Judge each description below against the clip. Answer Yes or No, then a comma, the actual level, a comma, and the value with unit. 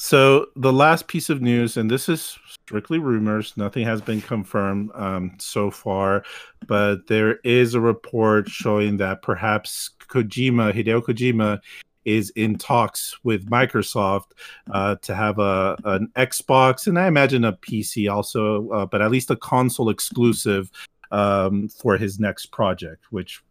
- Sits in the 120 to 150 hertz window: No, low, 110 Hz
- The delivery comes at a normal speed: Yes, average, 150 wpm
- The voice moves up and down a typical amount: Yes, average, 3.3 semitones